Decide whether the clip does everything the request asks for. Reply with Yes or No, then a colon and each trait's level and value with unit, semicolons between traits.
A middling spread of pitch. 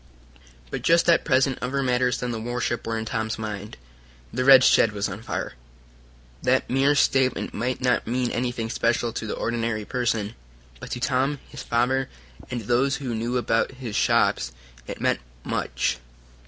No: narrow, 2.3 semitones